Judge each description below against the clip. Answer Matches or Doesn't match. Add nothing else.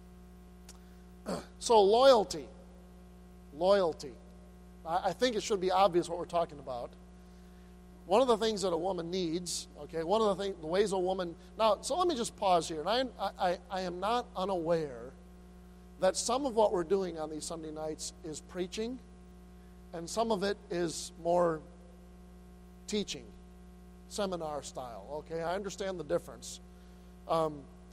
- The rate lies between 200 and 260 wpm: Doesn't match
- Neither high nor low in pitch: Matches